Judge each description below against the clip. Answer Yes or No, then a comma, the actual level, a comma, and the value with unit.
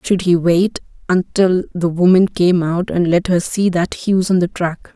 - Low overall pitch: No, medium, 180 Hz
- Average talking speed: No, fast, 220 wpm